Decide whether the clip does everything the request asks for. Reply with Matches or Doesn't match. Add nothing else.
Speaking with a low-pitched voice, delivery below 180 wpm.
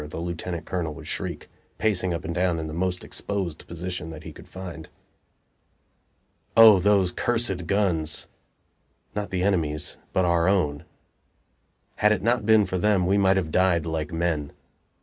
Matches